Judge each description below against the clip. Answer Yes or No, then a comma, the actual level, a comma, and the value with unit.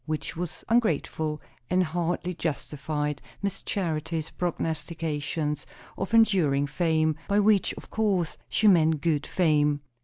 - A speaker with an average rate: No, slow, 120 wpm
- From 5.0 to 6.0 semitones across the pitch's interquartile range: No, average, 3.3 semitones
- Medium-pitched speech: Yes, medium, 160 Hz